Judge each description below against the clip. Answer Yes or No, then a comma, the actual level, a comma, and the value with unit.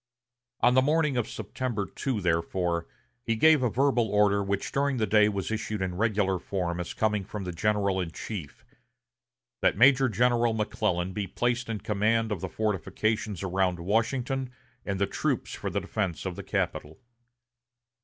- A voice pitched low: Yes, low, 105 Hz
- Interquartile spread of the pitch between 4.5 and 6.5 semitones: No, average, 3.9 semitones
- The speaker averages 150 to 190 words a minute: Yes, average, 165 wpm